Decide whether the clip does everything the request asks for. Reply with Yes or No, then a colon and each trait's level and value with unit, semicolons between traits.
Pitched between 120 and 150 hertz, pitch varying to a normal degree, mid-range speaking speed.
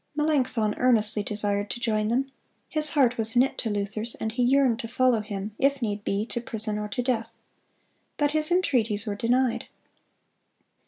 No: high, 230 Hz; average, 3.3 semitones; average, 170 wpm